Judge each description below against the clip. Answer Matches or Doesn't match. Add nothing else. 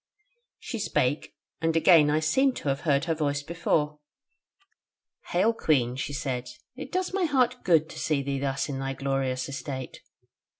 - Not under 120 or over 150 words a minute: Doesn't match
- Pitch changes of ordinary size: Matches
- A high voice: Doesn't match